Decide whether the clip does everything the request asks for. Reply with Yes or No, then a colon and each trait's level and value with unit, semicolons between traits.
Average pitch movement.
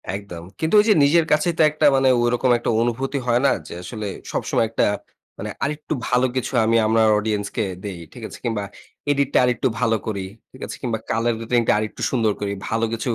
Yes: average, 3.5 semitones